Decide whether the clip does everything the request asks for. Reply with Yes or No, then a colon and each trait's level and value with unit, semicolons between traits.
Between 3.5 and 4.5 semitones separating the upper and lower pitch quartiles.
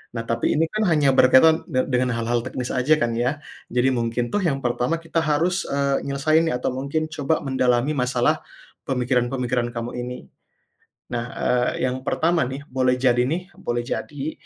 Yes: average, 3.8 semitones